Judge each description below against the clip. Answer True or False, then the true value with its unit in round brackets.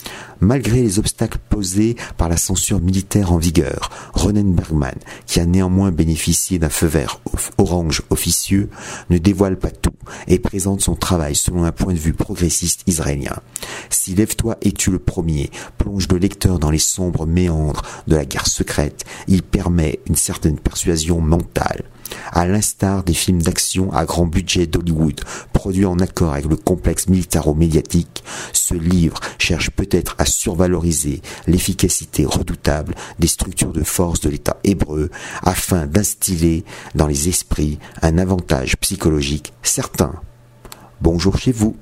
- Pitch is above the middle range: False (90 Hz)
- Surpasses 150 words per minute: False (145 wpm)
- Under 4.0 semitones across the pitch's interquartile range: True (3.0 semitones)